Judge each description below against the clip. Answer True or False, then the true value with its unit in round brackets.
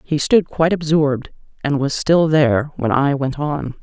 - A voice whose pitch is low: False (145 Hz)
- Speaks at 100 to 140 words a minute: False (190 wpm)